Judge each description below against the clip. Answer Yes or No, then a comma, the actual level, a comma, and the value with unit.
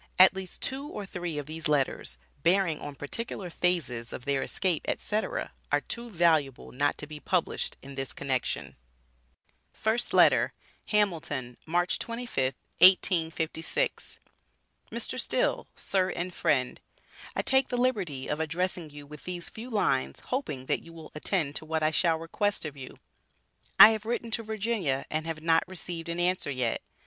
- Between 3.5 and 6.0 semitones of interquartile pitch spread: Yes, average, 5.2 semitones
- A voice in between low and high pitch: Yes, medium, 165 Hz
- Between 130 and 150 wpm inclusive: No, average, 160 wpm